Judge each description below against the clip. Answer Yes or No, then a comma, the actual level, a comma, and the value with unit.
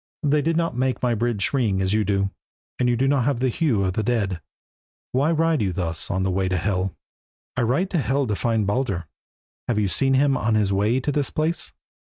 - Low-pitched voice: Yes, low, 120 Hz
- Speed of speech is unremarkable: No, fast, 230 wpm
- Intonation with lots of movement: Yes, wide, 5.7 semitones